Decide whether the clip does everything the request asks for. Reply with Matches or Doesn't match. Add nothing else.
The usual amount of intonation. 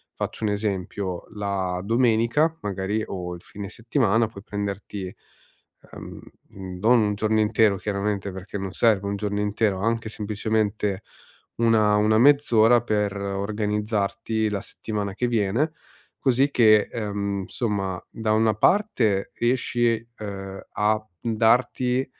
Doesn't match